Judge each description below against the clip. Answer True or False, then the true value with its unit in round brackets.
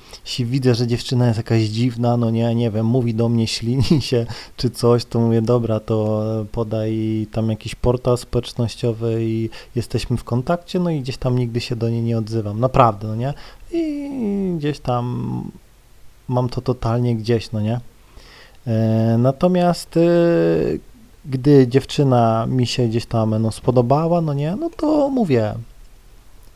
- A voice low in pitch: True (120 Hz)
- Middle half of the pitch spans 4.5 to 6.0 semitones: False (2.8 semitones)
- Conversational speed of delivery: True (150 wpm)